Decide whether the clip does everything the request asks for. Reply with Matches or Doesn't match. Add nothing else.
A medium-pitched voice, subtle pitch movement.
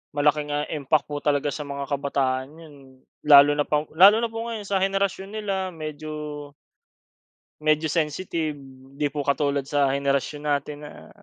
Matches